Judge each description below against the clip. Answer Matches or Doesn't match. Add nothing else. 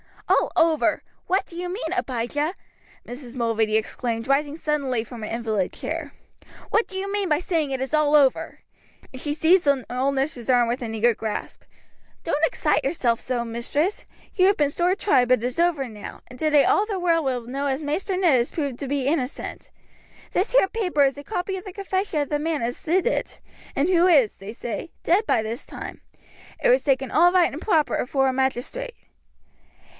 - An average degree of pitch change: Doesn't match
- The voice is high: Matches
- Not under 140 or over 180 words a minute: Doesn't match